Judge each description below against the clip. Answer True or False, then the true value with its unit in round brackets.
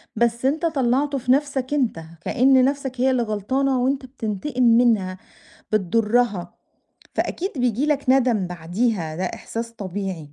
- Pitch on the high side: True (245 Hz)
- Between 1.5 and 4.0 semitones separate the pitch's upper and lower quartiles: False (4.5 semitones)